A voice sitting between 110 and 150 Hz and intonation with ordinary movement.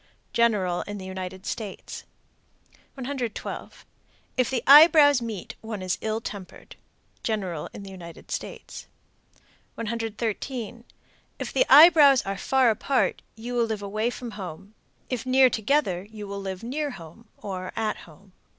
No: high, 220 Hz; average, 4.3 semitones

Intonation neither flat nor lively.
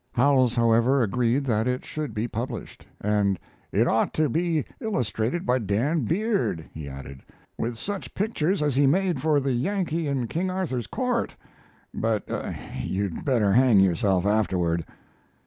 No: wide, 6.8 semitones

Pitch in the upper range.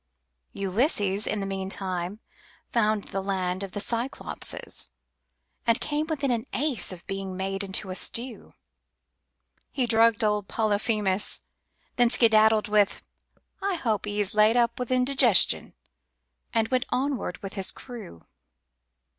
Yes: high, 215 Hz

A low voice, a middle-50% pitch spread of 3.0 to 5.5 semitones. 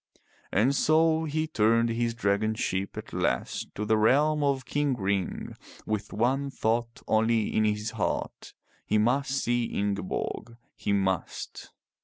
Yes: low, 115 Hz; average, 4.4 semitones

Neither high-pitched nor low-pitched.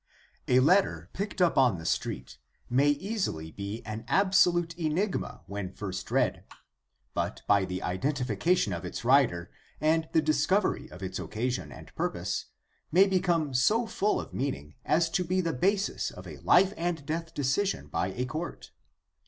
Yes: medium, 150 Hz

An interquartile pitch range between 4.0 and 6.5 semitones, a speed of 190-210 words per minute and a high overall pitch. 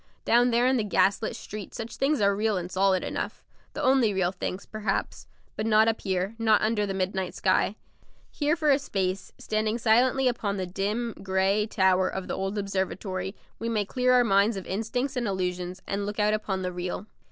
No: average, 3.1 semitones; average, 200 wpm; high, 205 Hz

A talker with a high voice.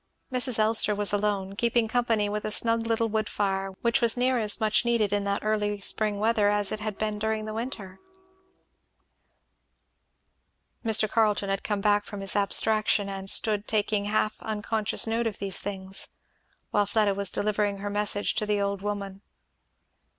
Yes: high, 210 Hz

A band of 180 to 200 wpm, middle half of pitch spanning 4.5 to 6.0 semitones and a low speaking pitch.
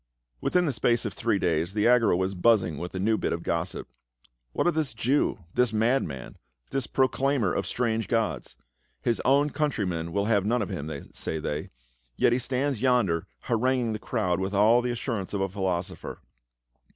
Yes: average, 190 wpm; average, 5.2 semitones; low, 110 Hz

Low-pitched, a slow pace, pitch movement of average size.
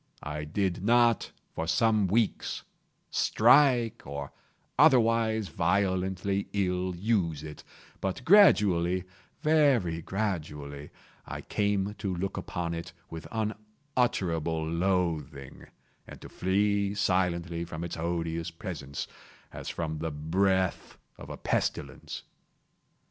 Yes: very low, 95 Hz; slow, 100 wpm; average, 4.1 semitones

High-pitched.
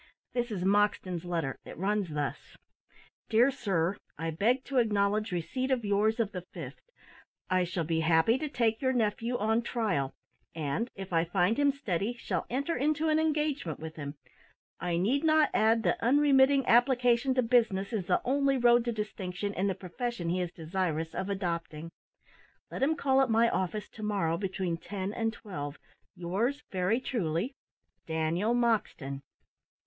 Yes: high, 205 Hz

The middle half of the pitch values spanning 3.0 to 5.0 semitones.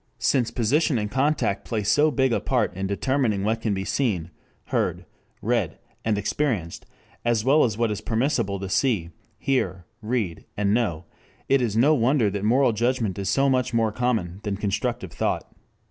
Yes: average, 4.4 semitones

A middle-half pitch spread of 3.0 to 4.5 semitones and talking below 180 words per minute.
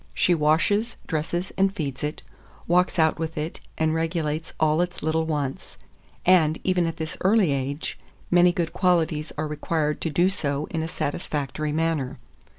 No: narrow, 2.5 semitones; average, 160 wpm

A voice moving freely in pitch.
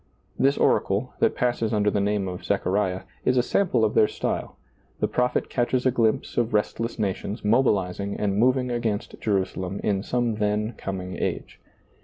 No: average, 3.3 semitones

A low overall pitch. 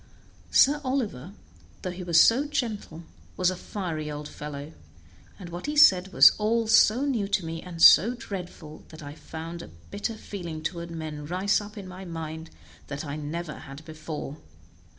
No: medium, 170 Hz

